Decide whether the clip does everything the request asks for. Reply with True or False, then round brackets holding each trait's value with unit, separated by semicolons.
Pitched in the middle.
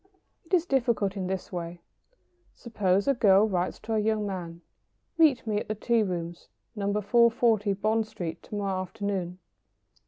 False (205 Hz)